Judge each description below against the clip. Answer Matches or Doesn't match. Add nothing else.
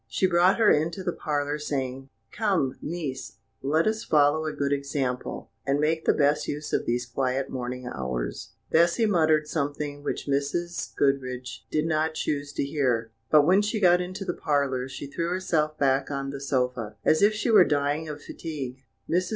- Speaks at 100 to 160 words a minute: Doesn't match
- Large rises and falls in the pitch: Doesn't match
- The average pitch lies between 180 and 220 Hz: Doesn't match